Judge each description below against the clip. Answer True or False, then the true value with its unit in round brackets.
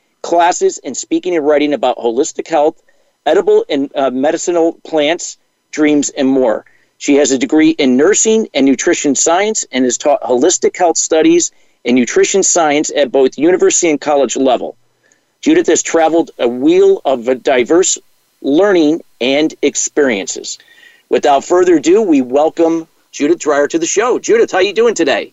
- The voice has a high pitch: True (210 Hz)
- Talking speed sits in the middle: True (160 wpm)